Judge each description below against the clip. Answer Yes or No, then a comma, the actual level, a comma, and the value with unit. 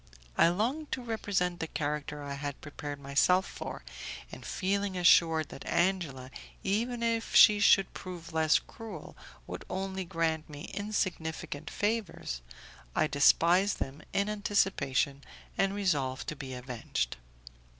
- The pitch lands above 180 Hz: No, medium, 170 Hz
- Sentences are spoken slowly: Yes, slow, 130 wpm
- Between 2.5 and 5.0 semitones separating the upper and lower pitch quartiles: No, wide, 5.6 semitones